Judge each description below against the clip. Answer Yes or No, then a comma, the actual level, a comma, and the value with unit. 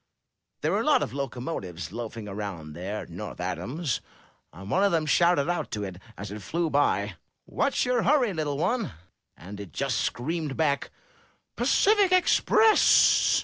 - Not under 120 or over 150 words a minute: No, average, 160 wpm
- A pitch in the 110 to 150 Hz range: Yes, medium, 140 Hz